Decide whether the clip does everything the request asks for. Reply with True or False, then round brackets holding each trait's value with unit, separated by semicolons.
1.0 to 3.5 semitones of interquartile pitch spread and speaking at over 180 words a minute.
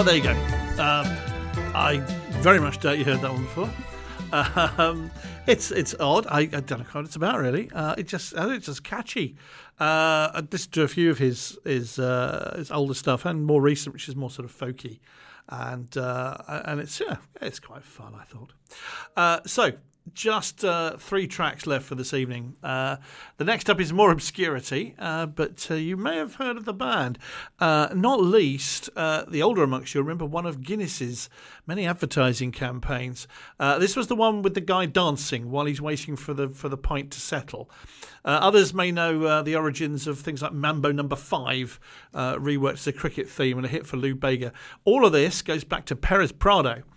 False (4.0 semitones; 200 wpm)